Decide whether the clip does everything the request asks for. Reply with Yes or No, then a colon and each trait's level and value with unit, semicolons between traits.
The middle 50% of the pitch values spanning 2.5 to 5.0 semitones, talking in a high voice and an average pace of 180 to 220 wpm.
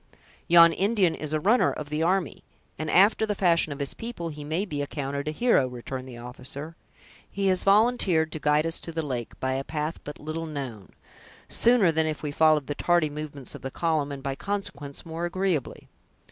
No: average, 3.4 semitones; medium, 155 Hz; average, 200 wpm